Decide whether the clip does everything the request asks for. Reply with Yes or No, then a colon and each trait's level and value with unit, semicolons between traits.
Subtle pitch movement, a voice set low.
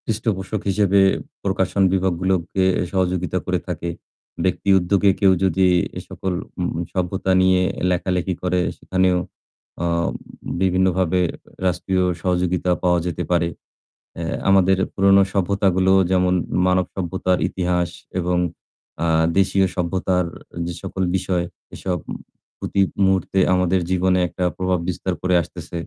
Yes: narrow, 1.0 semitones; very low, 95 Hz